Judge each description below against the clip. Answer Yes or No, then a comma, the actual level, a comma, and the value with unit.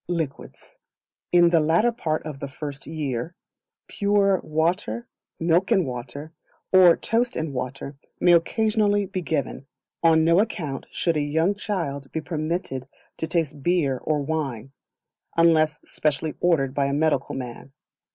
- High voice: No, medium, 160 Hz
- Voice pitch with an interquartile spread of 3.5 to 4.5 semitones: Yes, average, 4.0 semitones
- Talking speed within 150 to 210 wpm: No, average, 140 wpm